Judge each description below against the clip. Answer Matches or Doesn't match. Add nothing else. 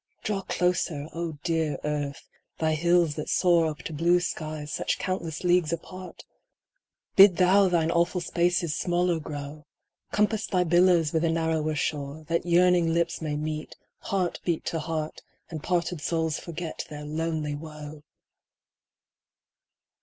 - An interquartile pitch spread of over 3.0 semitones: Doesn't match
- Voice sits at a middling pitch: Matches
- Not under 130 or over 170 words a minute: Matches